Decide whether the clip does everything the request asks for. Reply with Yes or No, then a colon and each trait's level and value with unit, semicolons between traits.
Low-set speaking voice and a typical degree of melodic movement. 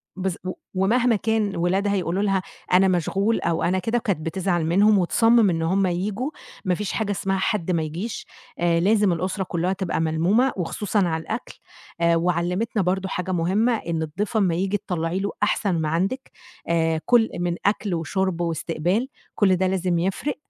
No: medium, 185 Hz; average, 3.2 semitones